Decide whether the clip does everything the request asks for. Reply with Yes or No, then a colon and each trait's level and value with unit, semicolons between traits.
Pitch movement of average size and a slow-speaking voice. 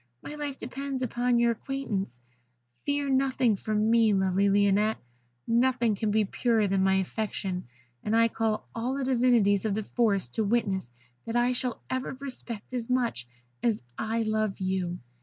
No: average, 3.7 semitones; average, 160 wpm